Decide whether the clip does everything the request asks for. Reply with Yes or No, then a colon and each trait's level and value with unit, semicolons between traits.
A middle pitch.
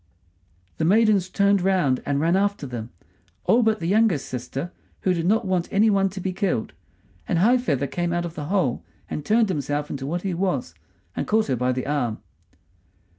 Yes: medium, 175 Hz